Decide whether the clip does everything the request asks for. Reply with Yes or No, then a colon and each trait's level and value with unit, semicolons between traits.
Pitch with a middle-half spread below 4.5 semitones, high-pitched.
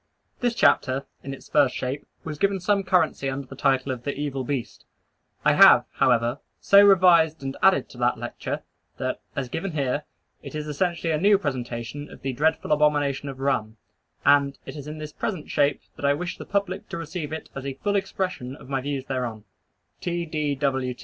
No: average, 3.8 semitones; medium, 145 Hz